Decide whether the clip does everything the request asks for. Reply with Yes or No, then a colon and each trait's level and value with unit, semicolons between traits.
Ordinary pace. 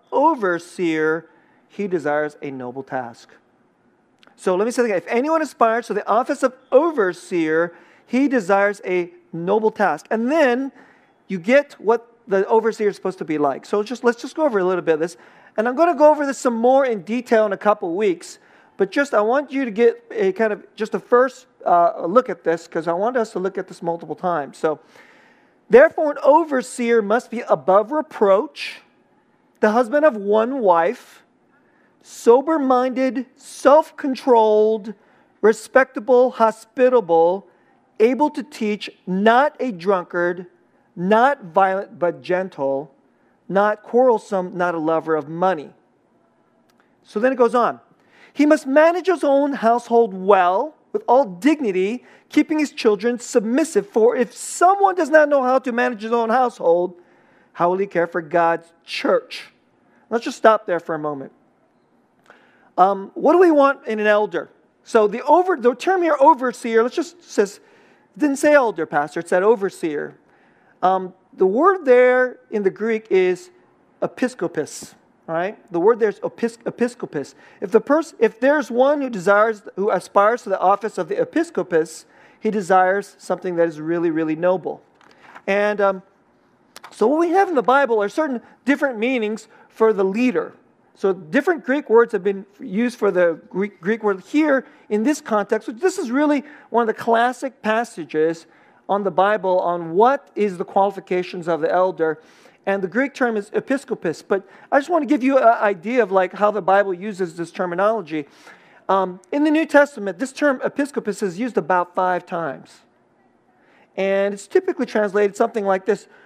Yes: average, 170 wpm